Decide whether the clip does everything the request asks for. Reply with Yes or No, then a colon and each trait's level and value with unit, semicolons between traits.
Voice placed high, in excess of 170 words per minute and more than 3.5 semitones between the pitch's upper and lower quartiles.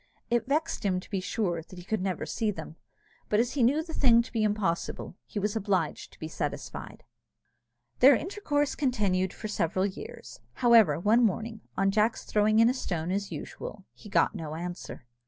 Yes: high, 210 Hz; average, 190 wpm; average, 4.3 semitones